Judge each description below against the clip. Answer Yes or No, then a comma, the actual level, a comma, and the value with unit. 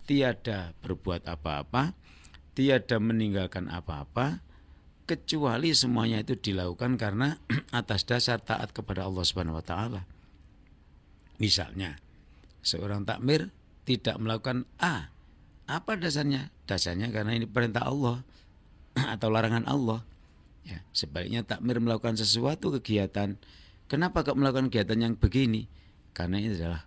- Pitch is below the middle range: Yes, low, 110 Hz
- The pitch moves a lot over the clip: Yes, wide, 6.0 semitones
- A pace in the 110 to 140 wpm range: Yes, average, 115 wpm